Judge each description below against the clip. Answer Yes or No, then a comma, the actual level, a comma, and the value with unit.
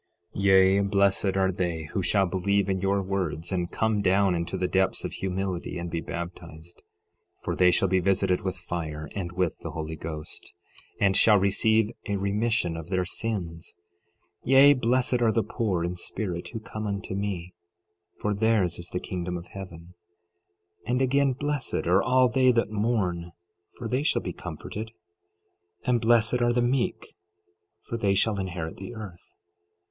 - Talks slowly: No, average, 175 wpm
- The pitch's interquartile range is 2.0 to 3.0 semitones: No, average, 4.0 semitones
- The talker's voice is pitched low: Yes, very low, 95 Hz